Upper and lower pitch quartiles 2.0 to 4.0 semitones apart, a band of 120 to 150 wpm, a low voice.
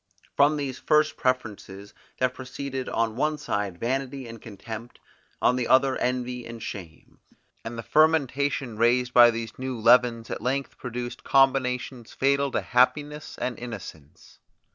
Yes: average, 2.8 semitones; average, 140 wpm; low, 125 Hz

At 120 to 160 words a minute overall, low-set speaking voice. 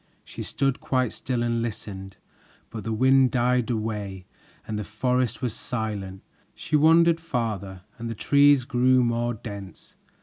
Yes: average, 145 wpm; low, 120 Hz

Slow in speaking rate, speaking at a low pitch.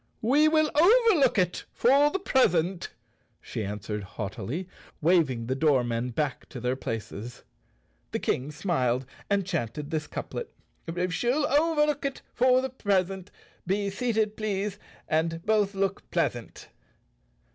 No: slow, 130 wpm; medium, 185 Hz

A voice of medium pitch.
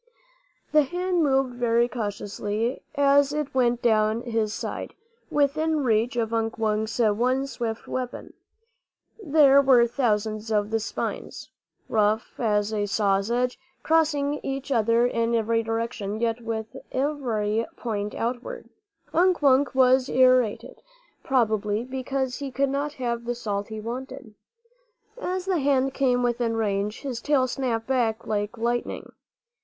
No: high, 240 Hz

